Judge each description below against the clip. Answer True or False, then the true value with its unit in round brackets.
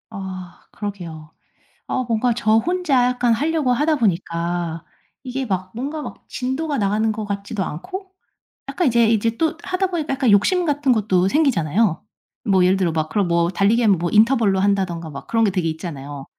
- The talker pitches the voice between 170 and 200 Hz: False (215 Hz)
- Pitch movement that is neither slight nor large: False (6.3 semitones)